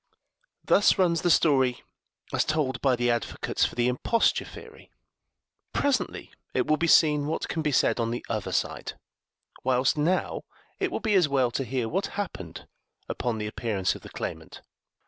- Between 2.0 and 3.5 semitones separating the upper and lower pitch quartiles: No, average, 5.3 semitones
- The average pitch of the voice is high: No, low, 135 Hz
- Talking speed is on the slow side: No, average, 170 wpm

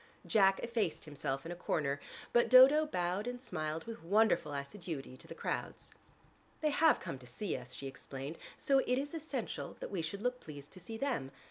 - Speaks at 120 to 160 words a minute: No, average, 195 wpm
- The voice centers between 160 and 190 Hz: Yes, medium, 185 Hz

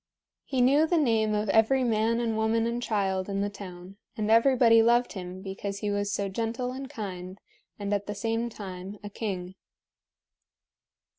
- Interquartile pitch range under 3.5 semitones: Yes, average, 2.8 semitones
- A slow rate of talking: No, average, 170 wpm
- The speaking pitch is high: Yes, high, 215 Hz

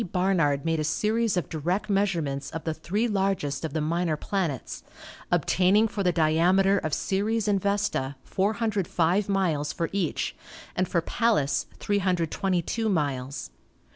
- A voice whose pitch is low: No, medium, 180 Hz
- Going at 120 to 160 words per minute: Yes, average, 140 wpm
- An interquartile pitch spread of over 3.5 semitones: Yes, average, 4.2 semitones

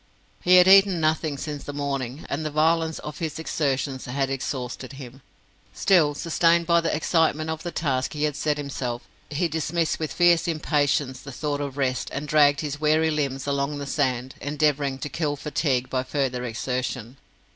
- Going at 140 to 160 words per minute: No, average, 180 wpm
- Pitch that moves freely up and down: No, average, 2.8 semitones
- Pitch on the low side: No, medium, 145 Hz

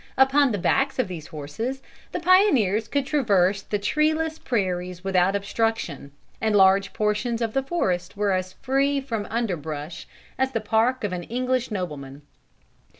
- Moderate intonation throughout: No, wide, 6.2 semitones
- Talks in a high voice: Yes, high, 215 Hz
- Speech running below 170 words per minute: Yes, average, 150 wpm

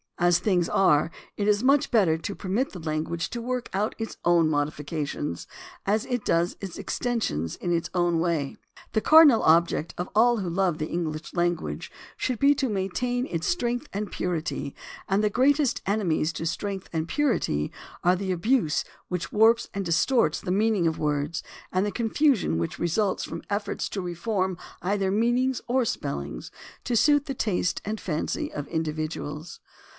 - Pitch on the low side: No, medium, 185 Hz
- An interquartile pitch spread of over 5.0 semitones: Yes, wide, 5.6 semitones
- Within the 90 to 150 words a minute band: No, average, 170 wpm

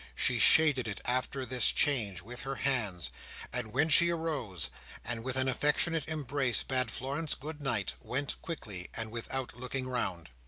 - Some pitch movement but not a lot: Yes, average, 3.9 semitones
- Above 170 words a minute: No, average, 160 wpm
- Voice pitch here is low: Yes, low, 130 Hz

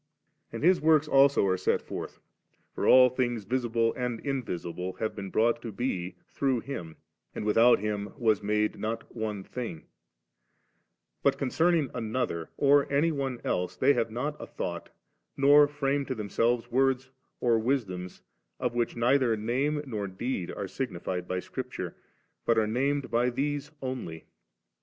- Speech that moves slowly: No, average, 150 wpm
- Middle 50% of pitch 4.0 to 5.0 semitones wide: Yes, average, 4.4 semitones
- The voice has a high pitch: No, low, 120 Hz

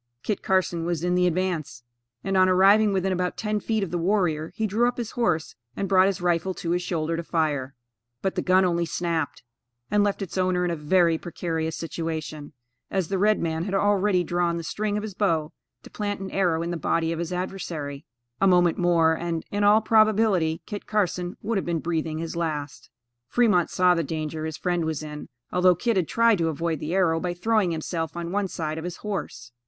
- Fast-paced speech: Yes, fast, 215 wpm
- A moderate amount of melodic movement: Yes, average, 3.0 semitones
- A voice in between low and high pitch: Yes, medium, 175 Hz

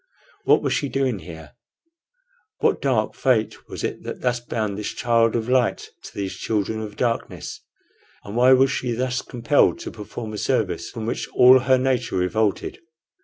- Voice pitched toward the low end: Yes, low, 115 Hz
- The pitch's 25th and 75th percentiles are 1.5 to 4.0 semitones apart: Yes, average, 2.9 semitones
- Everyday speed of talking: Yes, average, 170 wpm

